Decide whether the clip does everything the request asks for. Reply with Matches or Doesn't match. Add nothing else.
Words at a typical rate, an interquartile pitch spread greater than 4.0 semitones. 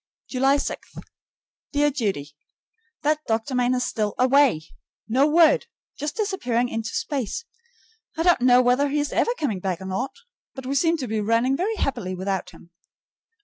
Matches